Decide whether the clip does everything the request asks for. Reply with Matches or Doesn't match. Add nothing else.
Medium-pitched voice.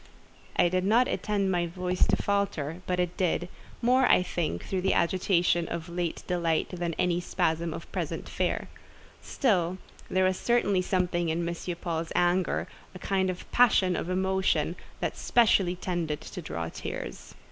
Matches